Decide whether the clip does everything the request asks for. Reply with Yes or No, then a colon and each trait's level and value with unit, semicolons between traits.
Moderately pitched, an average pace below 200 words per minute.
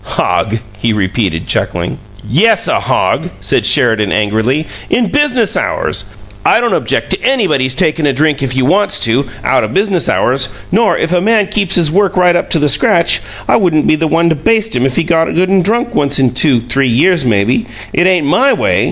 No: medium, 160 Hz; fast, 205 wpm